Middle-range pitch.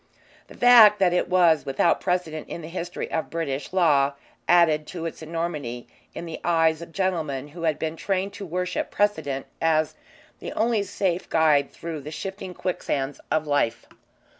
Yes: medium, 165 Hz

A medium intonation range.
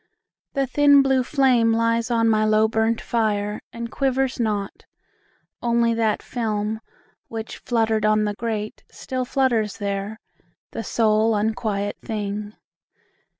No: narrow, 1.8 semitones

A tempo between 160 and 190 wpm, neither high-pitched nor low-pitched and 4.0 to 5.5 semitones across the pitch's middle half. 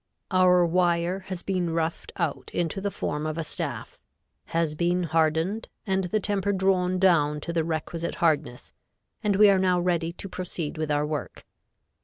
No: average, 170 wpm; medium, 175 Hz; average, 2.7 semitones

